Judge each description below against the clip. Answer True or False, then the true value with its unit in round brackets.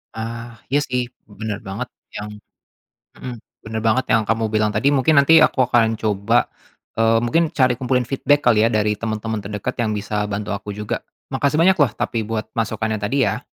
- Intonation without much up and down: False (3.0 semitones)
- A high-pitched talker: False (115 Hz)